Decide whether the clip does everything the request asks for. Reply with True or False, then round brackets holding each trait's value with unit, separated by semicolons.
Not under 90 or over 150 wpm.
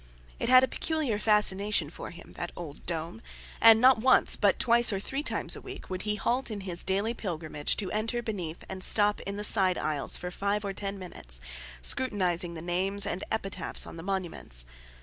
False (195 wpm)